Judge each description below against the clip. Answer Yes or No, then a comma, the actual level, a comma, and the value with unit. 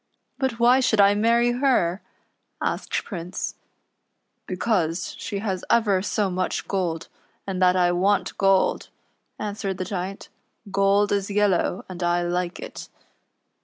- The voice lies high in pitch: Yes, high, 195 Hz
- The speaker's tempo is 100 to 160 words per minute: Yes, average, 150 wpm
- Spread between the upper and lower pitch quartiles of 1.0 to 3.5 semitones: Yes, narrow, 2.6 semitones